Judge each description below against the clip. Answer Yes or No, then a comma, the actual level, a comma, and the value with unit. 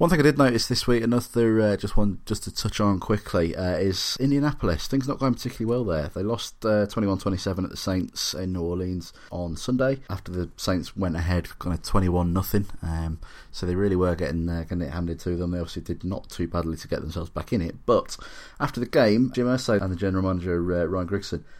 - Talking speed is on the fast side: Yes, fast, 230 wpm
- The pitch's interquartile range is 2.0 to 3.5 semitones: No, average, 4.2 semitones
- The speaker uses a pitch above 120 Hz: No, very low, 95 Hz